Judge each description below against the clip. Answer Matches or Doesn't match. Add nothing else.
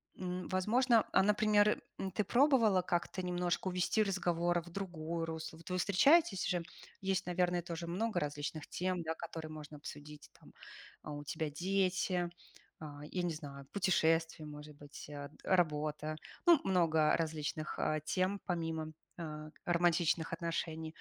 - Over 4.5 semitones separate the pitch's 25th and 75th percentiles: Doesn't match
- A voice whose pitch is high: Doesn't match